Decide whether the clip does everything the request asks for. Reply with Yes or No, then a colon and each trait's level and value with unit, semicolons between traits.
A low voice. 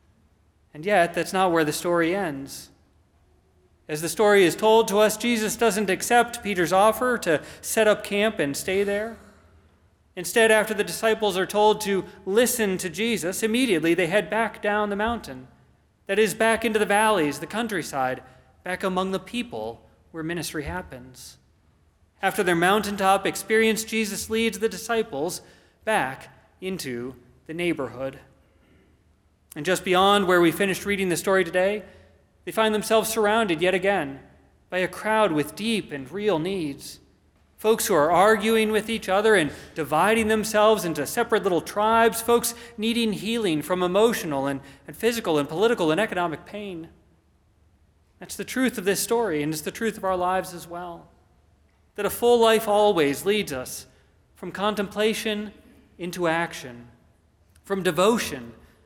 No: medium, 185 Hz